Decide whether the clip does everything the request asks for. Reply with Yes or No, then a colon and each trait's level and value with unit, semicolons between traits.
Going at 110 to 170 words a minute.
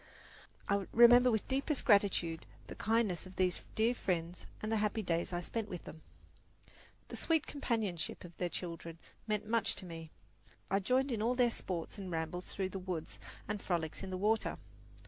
No: average, 180 wpm